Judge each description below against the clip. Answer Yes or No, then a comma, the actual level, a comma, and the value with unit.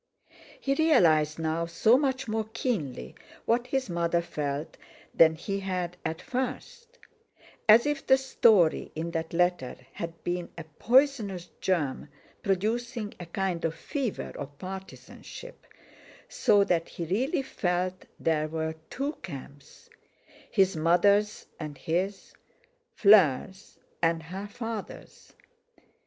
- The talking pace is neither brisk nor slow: No, slow, 115 wpm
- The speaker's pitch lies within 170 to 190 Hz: Yes, medium, 185 Hz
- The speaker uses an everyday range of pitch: No, wide, 6.1 semitones